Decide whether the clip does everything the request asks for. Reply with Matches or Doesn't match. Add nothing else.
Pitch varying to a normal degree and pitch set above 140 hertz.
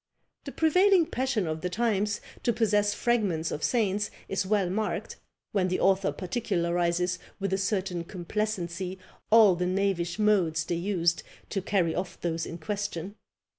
Matches